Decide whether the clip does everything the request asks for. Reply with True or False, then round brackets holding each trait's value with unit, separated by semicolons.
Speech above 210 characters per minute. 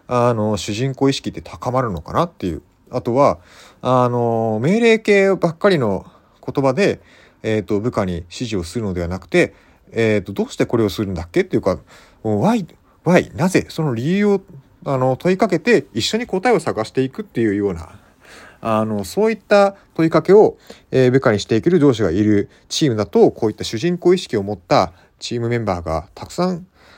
True (325 characters per minute)